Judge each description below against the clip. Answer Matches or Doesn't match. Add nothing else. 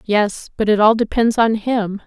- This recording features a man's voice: Doesn't match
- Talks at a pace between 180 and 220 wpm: Matches